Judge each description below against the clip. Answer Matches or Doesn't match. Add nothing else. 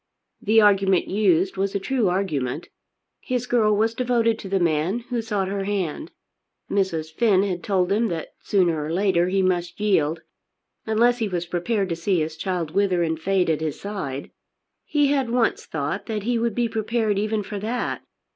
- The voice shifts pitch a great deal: Doesn't match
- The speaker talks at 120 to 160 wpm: Doesn't match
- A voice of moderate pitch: Doesn't match